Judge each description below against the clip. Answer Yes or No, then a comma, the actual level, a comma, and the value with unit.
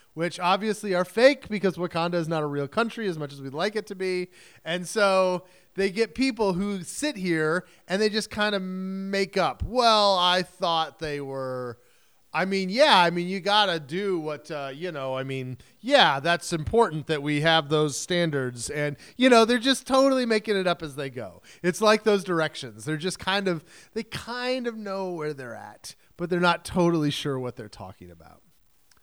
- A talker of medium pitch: Yes, medium, 180 Hz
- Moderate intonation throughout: Yes, average, 4.9 semitones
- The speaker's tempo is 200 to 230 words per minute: Yes, fast, 205 wpm